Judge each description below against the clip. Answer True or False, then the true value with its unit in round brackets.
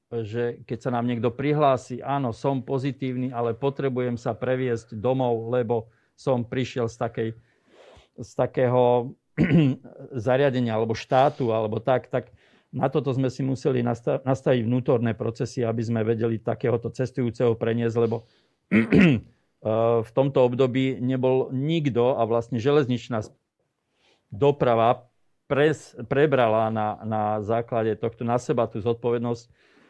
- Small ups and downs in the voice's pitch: True (2.2 semitones)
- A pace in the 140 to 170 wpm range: False (120 wpm)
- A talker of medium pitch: False (120 Hz)